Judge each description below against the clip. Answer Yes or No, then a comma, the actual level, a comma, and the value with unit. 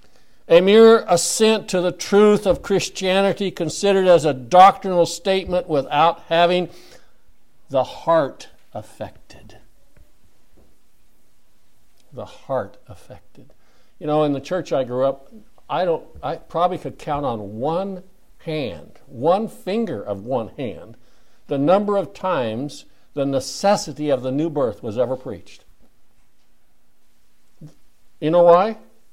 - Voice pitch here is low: No, medium, 180 Hz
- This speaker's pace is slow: Yes, slow, 120 wpm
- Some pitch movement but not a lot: Yes, average, 3.7 semitones